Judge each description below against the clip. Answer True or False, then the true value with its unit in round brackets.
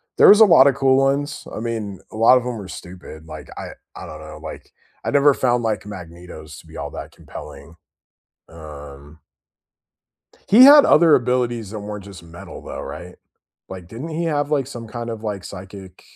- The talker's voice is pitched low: True (110 Hz)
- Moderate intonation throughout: False (7.3 semitones)